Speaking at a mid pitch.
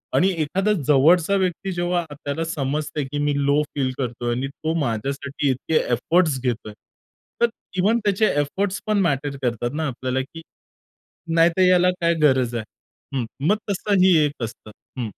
Yes: medium, 145 Hz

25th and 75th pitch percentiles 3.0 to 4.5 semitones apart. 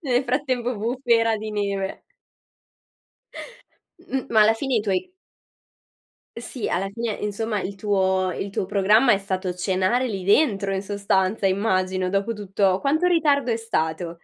Yes: average, 3.6 semitones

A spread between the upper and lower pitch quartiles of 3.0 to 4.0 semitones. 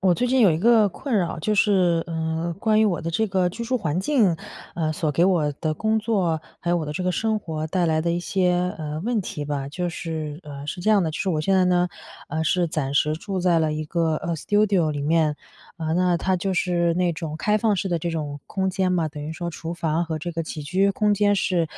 Yes: average, 3.3 semitones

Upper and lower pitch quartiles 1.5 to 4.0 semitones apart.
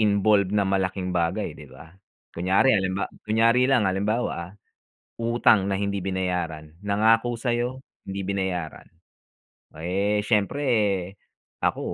Yes: average, 3.0 semitones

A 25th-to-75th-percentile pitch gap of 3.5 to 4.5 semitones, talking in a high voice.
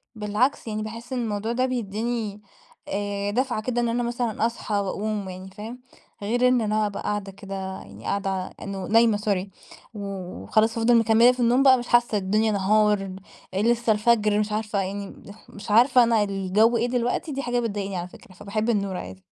No: average, 2.9 semitones; high, 215 Hz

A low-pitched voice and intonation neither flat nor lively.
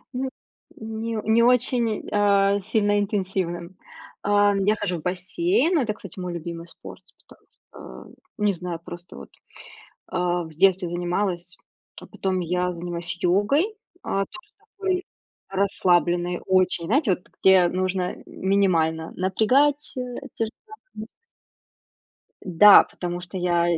No: high, 190 Hz; average, 3.4 semitones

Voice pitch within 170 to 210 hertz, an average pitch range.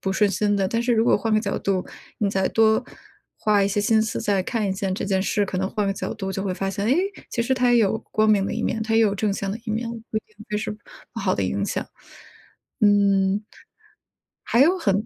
No: high, 205 Hz; narrow, 2.2 semitones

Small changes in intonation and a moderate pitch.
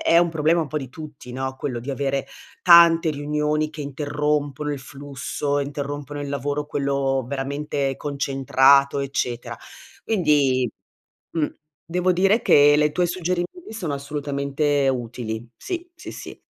Yes: narrow, 1.9 semitones; medium, 145 Hz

